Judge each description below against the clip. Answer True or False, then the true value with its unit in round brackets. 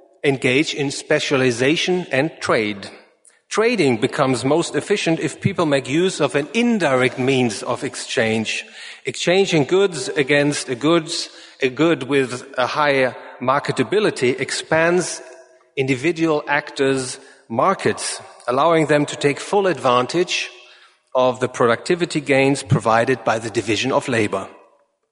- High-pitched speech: False (140 Hz)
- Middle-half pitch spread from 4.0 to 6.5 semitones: True (4.4 semitones)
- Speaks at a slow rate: True (120 wpm)